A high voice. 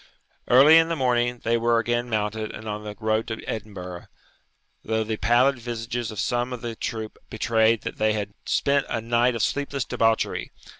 No: low, 115 Hz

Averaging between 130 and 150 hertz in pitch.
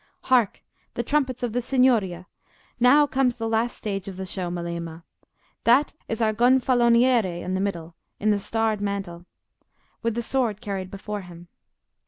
No: high, 215 Hz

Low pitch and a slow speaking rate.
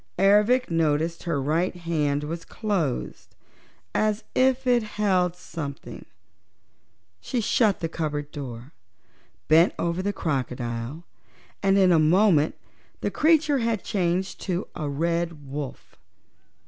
No: medium, 170 Hz; slow, 125 wpm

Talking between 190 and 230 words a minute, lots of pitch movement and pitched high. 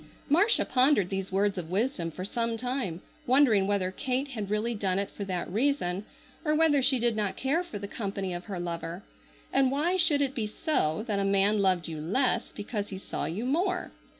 Yes: fast, 205 wpm; wide, 5.8 semitones; high, 210 Hz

